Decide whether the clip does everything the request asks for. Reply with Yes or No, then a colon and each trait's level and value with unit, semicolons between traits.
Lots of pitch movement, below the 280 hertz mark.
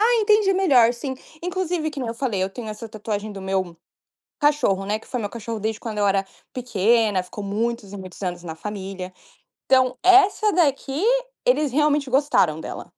Yes: wide, 6.7 semitones; high, 230 Hz